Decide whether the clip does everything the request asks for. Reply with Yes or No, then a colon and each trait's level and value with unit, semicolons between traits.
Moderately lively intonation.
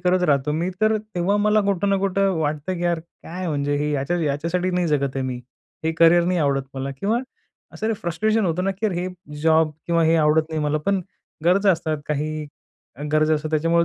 Yes: average, 3.5 semitones